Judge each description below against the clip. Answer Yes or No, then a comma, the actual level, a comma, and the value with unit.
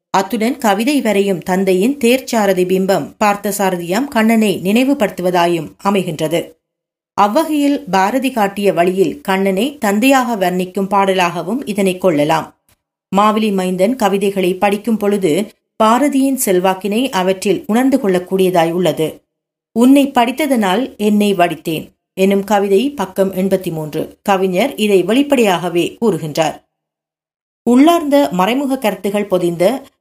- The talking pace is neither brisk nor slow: Yes, average, 95 wpm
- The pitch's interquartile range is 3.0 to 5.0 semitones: Yes, average, 3.7 semitones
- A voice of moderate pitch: No, high, 200 Hz